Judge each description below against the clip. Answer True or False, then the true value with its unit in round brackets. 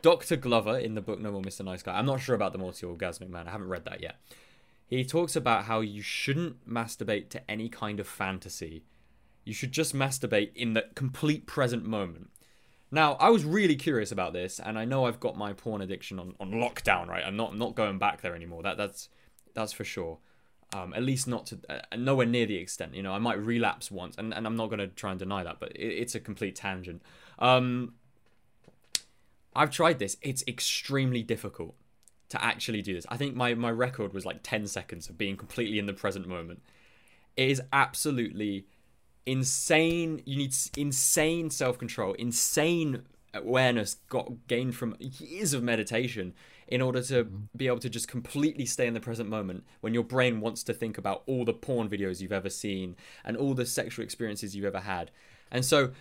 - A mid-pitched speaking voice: False (115 Hz)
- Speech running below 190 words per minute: False (200 wpm)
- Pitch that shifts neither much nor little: True (4.1 semitones)